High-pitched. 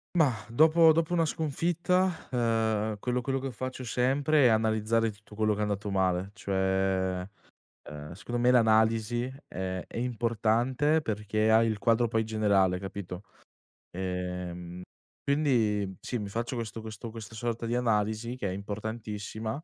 No: low, 110 Hz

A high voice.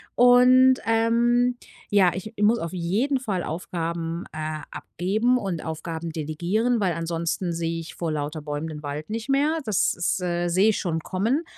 No: medium, 180 Hz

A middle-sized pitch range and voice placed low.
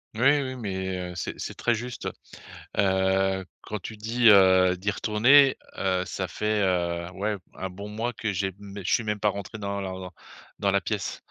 No: narrow, 2.3 semitones; low, 100 Hz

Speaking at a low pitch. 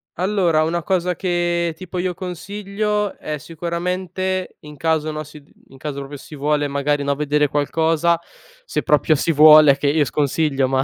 No: medium, 155 Hz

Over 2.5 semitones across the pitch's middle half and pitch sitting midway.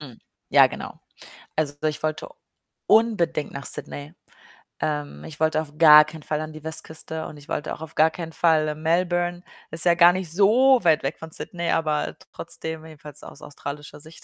No: narrow, 1.9 semitones; medium, 155 Hz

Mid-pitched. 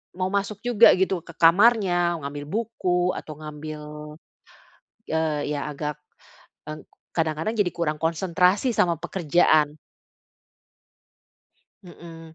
Yes: medium, 170 Hz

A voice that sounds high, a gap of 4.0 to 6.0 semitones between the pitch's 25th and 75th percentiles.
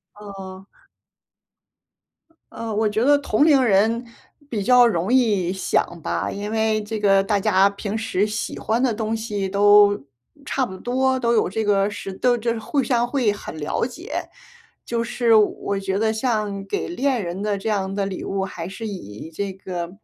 No: high, 210 Hz; average, 3.0 semitones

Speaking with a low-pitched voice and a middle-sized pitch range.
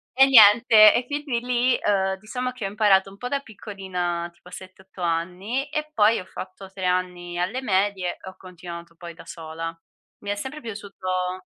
No: high, 195 Hz; average, 4.3 semitones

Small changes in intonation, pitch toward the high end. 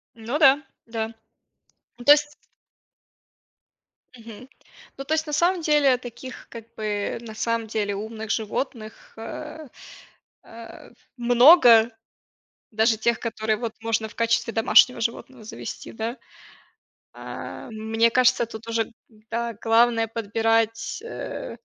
Yes: narrow, 2.2 semitones; high, 230 Hz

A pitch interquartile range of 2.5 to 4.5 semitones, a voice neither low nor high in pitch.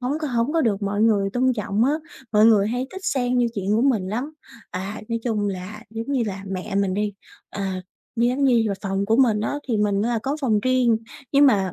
No: average, 3.8 semitones; high, 220 Hz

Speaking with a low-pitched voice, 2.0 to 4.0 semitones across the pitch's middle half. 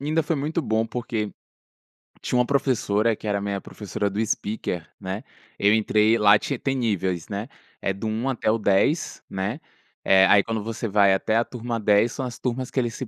Yes: low, 110 Hz; average, 3.3 semitones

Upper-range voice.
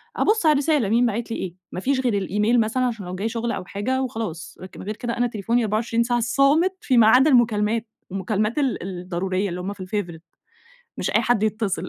Yes: high, 225 Hz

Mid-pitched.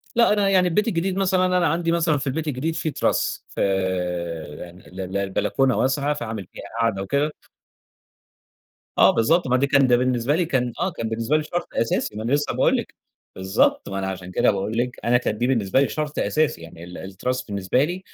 No: low, 130 Hz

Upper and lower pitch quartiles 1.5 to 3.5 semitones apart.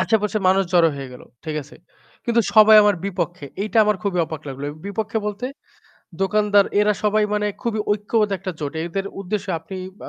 Yes: average, 3.0 semitones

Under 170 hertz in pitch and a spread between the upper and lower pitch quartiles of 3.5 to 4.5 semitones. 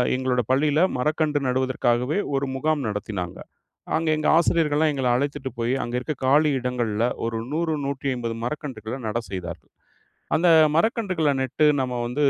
Yes: low, 135 Hz; average, 4.1 semitones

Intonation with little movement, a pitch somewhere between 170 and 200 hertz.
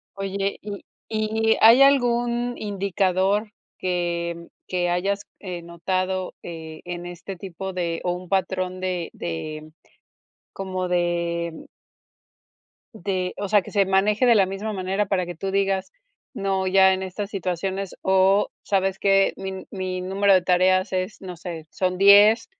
Yes: narrow, 1.8 semitones; high, 190 Hz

